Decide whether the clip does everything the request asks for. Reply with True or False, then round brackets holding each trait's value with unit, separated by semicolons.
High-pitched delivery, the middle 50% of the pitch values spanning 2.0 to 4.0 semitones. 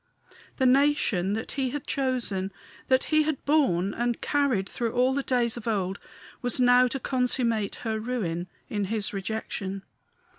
False (240 Hz; 4.4 semitones)